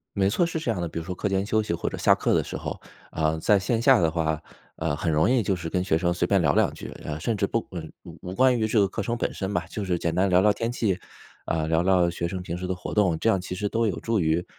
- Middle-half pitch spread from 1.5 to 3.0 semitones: No, average, 4.0 semitones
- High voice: No, very low, 95 Hz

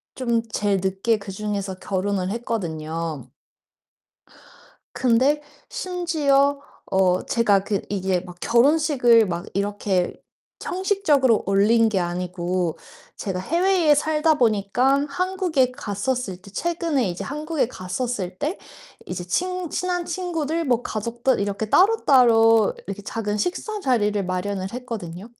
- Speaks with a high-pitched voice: Yes, high, 230 Hz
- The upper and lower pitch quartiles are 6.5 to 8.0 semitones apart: Yes, wide, 7.3 semitones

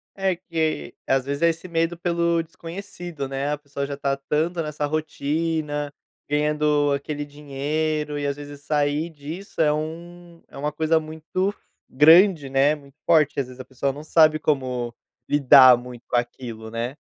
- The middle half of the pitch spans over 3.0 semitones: No, average, 2.7 semitones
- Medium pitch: Yes, medium, 150 Hz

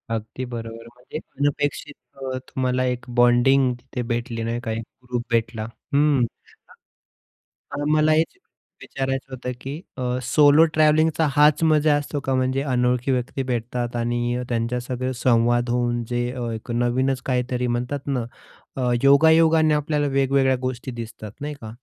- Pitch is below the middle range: Yes, low, 130 Hz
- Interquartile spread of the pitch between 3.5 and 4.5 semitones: No, average, 3.0 semitones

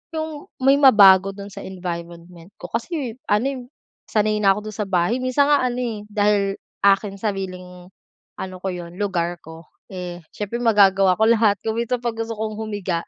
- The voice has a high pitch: Yes, high, 205 Hz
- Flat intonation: No, average, 3.6 semitones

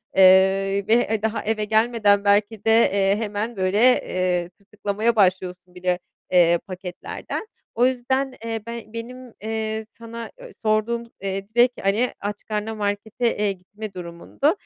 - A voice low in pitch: No, high, 210 Hz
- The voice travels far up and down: No, average, 2.9 semitones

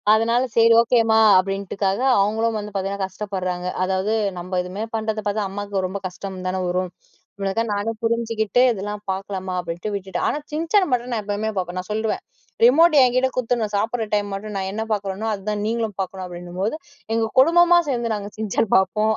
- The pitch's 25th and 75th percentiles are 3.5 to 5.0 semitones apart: No, average, 3.0 semitones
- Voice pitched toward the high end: Yes, high, 210 Hz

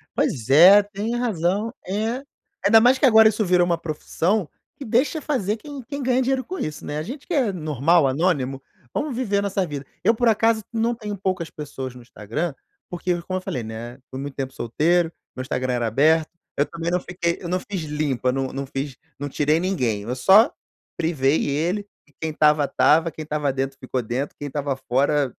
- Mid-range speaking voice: Yes, medium, 165 Hz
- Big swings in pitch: Yes, wide, 7.1 semitones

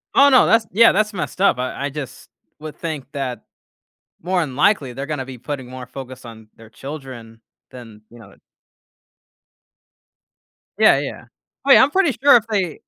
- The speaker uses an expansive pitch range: Yes, wide, 7.4 semitones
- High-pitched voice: No, medium, 140 Hz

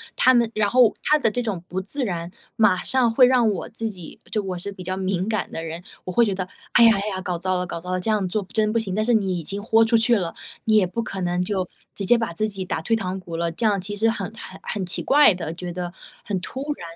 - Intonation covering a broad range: No, average, 3.6 semitones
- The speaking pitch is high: Yes, high, 200 Hz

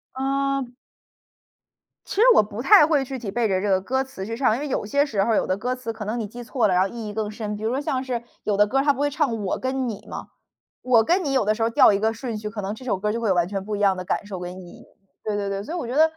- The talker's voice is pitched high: Yes, high, 225 Hz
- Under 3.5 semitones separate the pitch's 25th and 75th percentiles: No, average, 4.3 semitones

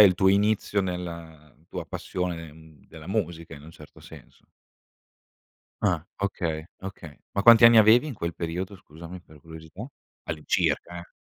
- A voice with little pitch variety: No, average, 3.6 semitones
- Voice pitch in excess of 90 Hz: No, very low, 85 Hz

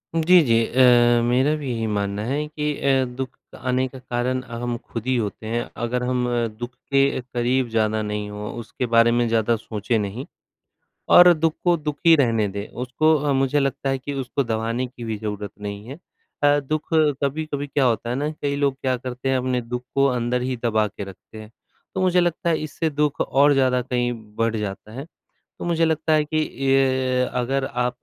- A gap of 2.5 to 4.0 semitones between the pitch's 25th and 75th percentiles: Yes, average, 3.4 semitones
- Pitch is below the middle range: Yes, low, 125 Hz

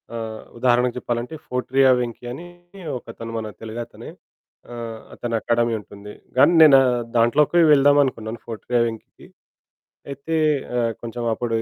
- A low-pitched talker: Yes, low, 120 Hz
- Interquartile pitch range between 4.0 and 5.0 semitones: No, narrow, 2.4 semitones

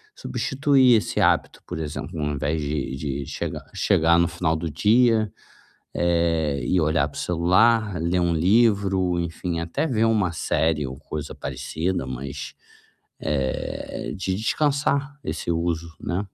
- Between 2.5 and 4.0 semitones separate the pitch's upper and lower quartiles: No, average, 5.0 semitones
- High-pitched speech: No, very low, 85 Hz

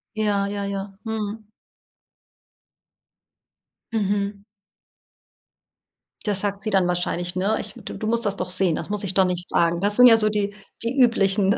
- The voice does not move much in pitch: Yes, narrow, 1.8 semitones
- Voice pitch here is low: No, high, 200 Hz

